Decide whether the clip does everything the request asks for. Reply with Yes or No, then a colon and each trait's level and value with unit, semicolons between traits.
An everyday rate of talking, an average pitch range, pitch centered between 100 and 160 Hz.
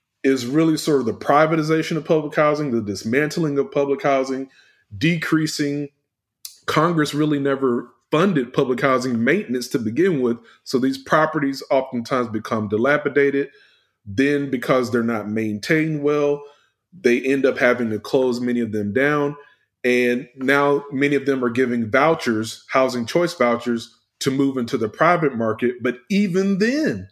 Yes: average, 150 wpm; average, 3.5 semitones; low, 135 Hz